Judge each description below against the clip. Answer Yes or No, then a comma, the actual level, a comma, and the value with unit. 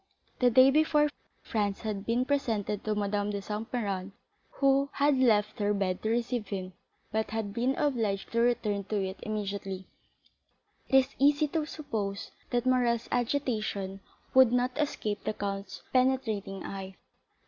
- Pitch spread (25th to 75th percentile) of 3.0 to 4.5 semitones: Yes, average, 4.2 semitones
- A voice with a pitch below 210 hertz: No, high, 220 Hz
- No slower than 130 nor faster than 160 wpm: Yes, average, 155 wpm